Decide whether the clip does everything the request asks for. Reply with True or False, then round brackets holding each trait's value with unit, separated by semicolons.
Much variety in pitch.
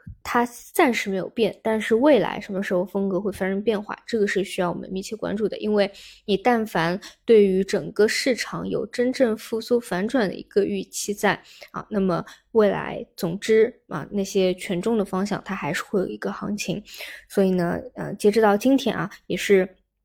False (2.7 semitones)